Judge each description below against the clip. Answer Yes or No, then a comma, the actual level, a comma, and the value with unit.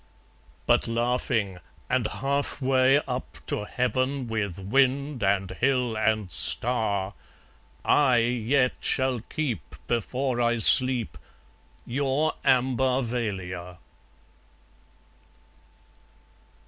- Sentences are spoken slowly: Yes, slow, 85 wpm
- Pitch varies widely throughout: No, average, 3.5 semitones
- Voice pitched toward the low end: Yes, low, 120 Hz